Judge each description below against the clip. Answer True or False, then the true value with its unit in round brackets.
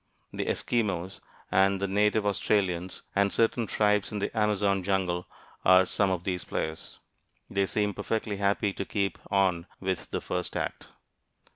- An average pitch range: False (1.8 semitones)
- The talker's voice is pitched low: True (100 Hz)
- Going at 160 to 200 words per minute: False (150 wpm)